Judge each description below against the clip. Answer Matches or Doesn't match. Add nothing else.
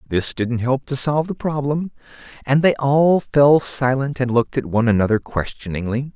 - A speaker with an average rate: Matches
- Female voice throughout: Doesn't match